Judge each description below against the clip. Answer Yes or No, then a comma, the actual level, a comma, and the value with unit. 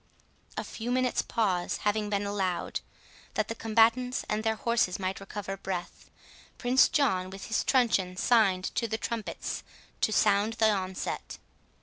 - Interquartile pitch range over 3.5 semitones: No, average, 3.0 semitones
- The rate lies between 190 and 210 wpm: No, average, 145 wpm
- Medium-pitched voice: No, high, 215 Hz